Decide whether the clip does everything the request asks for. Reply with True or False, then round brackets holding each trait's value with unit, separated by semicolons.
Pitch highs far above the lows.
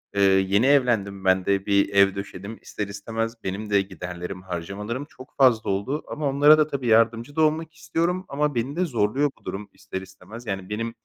True (6.0 semitones)